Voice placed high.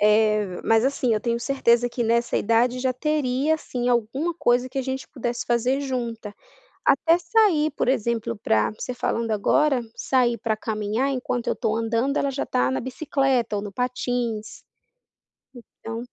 Yes: high, 245 Hz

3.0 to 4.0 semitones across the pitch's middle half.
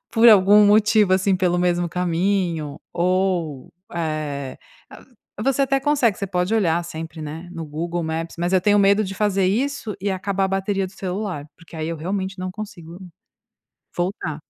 Yes: average, 3.3 semitones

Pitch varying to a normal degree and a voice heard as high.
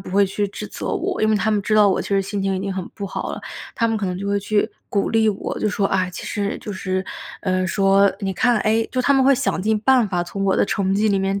No: narrow, 2.1 semitones; high, 200 Hz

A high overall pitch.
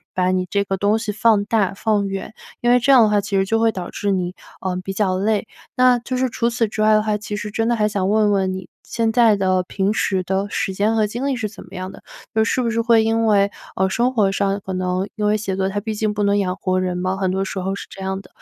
Yes: high, 205 Hz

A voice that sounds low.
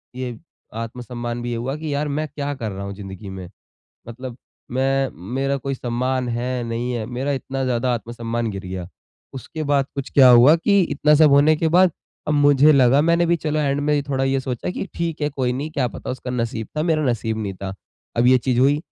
Yes: low, 130 Hz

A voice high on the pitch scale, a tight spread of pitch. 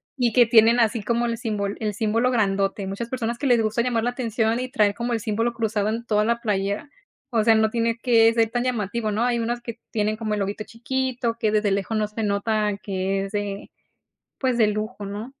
Yes: high, 225 Hz; narrow, 2.1 semitones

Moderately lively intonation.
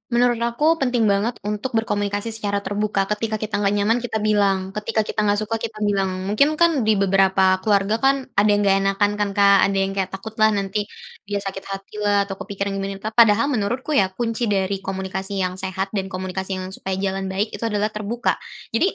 No: narrow, 2.0 semitones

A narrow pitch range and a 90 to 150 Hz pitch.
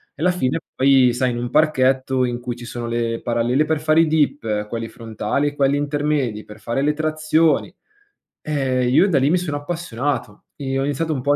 No: average, 4.0 semitones; low, 135 Hz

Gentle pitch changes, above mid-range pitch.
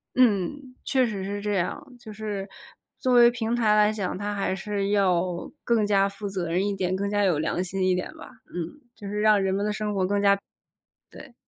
Yes: narrow, 2.0 semitones; high, 200 Hz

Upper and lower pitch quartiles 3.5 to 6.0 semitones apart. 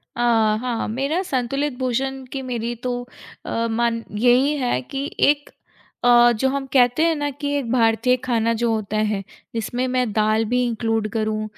No: average, 2.9 semitones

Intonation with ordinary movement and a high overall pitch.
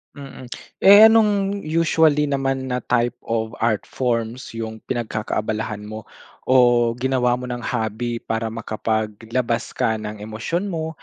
No: average, 3.5 semitones; low, 120 Hz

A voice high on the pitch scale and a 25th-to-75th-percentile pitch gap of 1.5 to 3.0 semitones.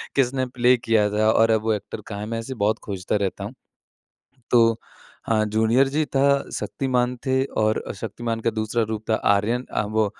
No: low, 115 Hz; narrow, 2.4 semitones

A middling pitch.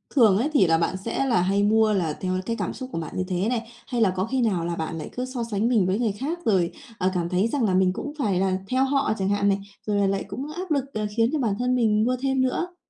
No: high, 215 Hz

